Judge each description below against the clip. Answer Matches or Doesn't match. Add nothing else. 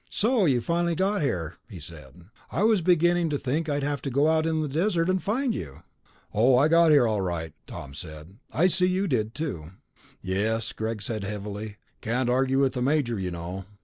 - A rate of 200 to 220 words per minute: Matches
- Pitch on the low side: Matches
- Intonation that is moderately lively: Doesn't match